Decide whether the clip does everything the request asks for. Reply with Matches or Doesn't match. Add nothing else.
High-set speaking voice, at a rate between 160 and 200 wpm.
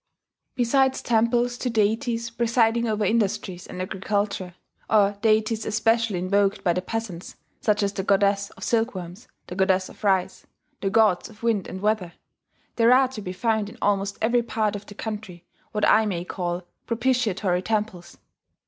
Matches